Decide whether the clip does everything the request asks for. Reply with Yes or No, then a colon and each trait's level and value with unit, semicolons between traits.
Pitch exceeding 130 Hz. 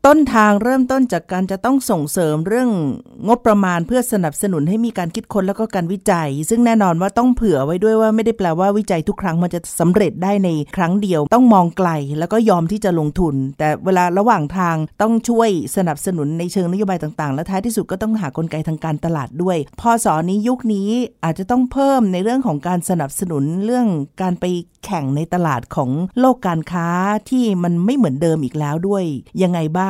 Yes: medium, 185 Hz